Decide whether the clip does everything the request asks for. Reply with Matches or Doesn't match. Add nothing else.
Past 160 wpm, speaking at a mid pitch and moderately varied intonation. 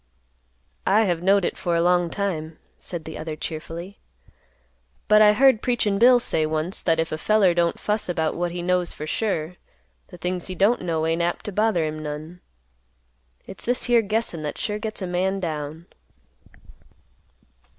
Matches